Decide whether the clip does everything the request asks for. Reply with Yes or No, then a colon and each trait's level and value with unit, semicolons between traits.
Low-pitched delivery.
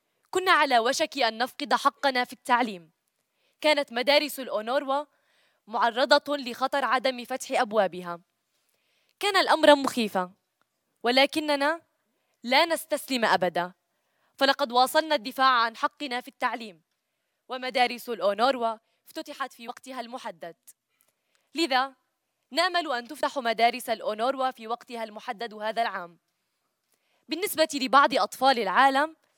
No: very high, 260 Hz